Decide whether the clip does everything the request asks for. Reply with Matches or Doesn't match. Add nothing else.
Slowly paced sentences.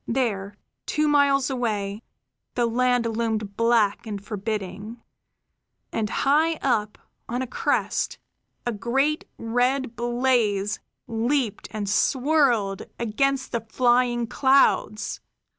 Matches